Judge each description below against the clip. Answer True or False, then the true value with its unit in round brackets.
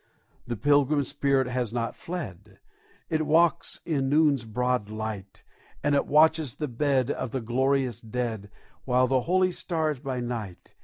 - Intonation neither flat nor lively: True (4.1 semitones)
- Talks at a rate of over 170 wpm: False (150 wpm)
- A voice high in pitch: False (130 Hz)